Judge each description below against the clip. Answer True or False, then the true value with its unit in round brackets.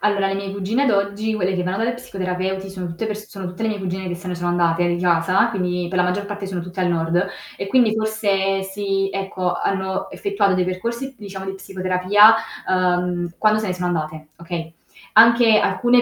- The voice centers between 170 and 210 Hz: True (190 Hz)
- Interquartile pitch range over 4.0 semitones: False (2.4 semitones)